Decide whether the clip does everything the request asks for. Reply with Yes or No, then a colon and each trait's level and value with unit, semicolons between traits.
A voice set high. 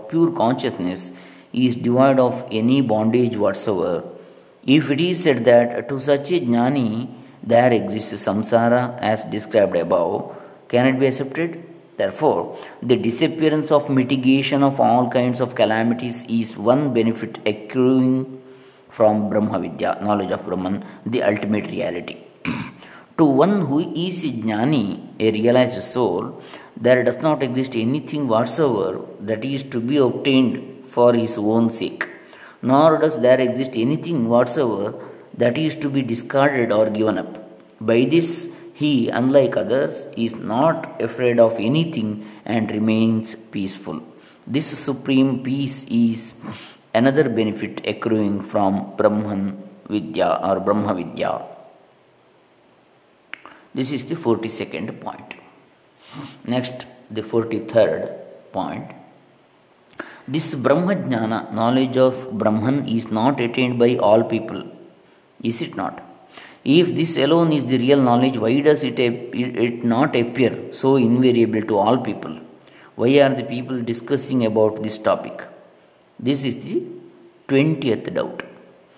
No: low, 125 Hz